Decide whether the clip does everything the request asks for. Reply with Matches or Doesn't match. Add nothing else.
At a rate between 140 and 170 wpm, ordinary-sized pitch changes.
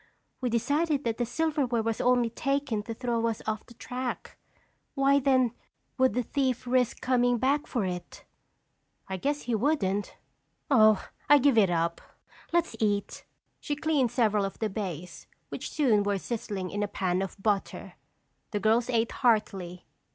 Matches